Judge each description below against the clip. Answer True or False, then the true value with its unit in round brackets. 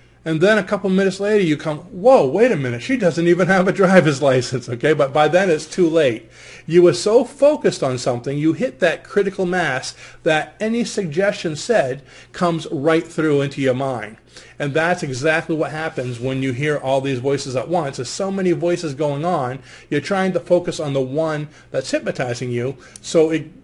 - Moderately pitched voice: True (160 Hz)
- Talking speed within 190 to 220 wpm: True (200 wpm)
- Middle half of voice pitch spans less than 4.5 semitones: False (5.1 semitones)